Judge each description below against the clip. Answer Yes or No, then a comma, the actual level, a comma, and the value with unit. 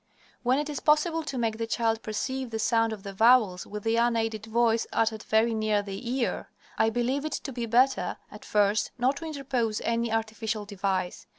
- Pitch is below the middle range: No, high, 225 Hz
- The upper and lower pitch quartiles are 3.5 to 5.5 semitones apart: No, average, 2.7 semitones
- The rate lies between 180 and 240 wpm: Yes, average, 195 wpm